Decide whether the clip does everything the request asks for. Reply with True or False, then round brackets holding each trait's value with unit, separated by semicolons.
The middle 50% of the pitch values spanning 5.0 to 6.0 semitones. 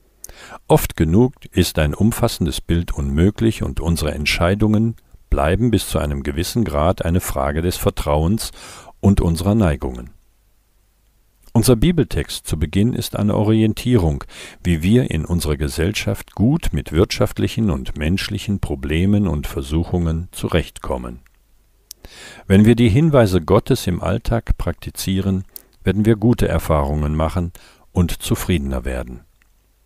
True (5.3 semitones)